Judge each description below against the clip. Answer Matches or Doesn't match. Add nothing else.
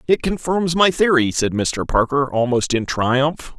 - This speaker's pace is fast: Doesn't match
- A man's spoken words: Matches